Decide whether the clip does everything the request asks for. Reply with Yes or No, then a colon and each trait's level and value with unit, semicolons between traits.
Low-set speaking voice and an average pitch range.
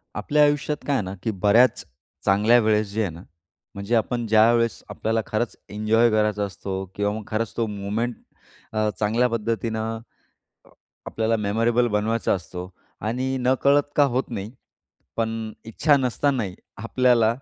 No: low, 110 Hz; narrow, 2.3 semitones